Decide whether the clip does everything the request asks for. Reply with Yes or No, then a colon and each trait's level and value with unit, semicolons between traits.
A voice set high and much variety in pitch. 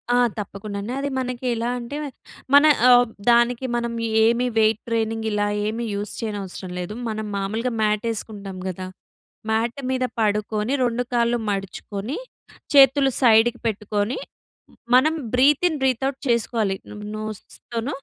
No: high, 225 Hz; average, 2.9 semitones